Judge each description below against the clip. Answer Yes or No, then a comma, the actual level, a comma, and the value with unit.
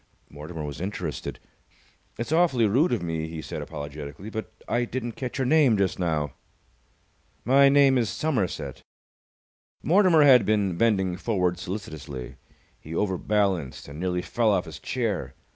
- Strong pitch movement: Yes, wide, 6.8 semitones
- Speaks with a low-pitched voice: Yes, low, 100 Hz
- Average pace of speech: Yes, average, 145 wpm